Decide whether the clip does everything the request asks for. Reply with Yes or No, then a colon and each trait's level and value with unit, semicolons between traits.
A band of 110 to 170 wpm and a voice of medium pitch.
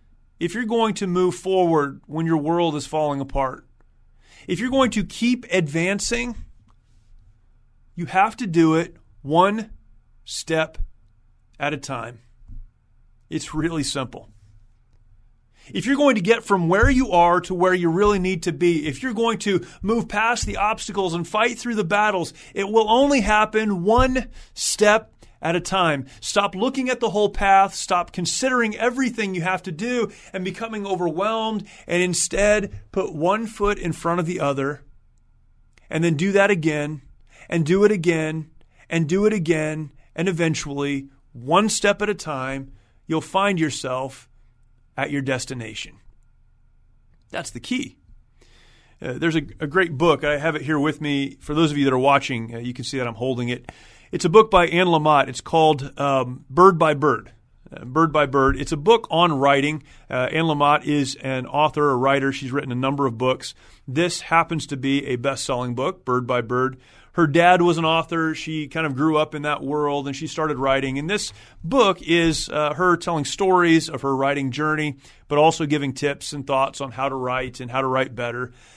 No: average, 185 wpm; medium, 155 Hz